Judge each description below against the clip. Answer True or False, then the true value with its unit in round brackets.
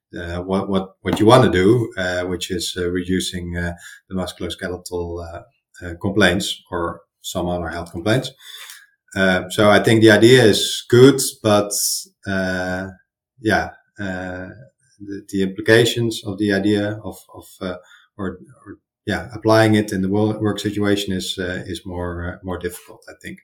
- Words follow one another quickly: False (160 wpm)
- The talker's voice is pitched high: False (95 Hz)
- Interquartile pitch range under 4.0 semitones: True (2.6 semitones)